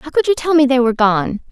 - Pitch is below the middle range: No, very high, 270 Hz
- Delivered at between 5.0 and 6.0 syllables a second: No, 6.4 syllables/s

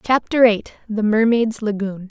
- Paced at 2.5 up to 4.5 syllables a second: Yes, 4.3 syllables/s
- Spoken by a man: No, female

